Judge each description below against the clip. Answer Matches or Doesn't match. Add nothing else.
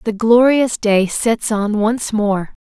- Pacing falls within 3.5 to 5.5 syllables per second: Doesn't match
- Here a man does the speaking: Doesn't match